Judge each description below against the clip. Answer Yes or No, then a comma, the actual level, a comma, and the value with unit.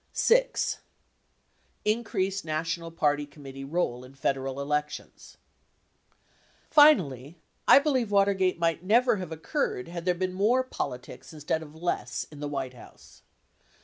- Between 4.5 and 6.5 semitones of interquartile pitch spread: Yes, wide, 5.5 semitones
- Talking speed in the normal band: No, slow, 125 wpm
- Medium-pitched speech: Yes, medium, 165 Hz